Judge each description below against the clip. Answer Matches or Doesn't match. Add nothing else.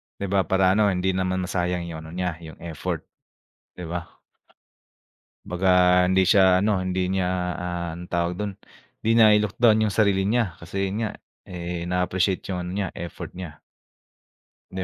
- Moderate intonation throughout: Doesn't match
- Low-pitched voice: Matches